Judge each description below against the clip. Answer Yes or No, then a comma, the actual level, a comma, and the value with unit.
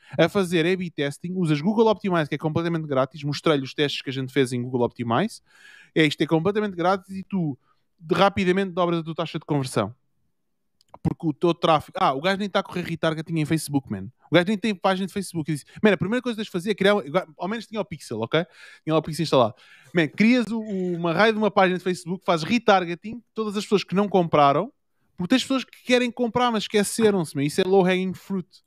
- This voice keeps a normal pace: No, fast, 230 wpm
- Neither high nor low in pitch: Yes, medium, 180 Hz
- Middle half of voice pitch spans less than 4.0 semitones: No, average, 4.4 semitones